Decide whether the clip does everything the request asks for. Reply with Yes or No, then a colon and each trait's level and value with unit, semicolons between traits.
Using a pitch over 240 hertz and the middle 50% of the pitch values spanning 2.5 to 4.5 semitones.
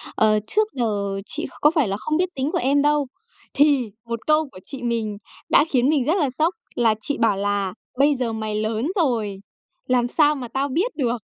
No: very high, 250 Hz; average, 5.3 semitones